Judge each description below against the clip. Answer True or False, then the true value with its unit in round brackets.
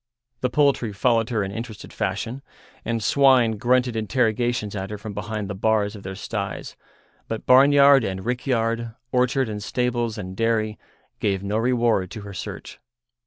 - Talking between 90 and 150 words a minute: False (160 wpm)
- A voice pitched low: True (115 Hz)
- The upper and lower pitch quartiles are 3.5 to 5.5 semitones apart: False (3.0 semitones)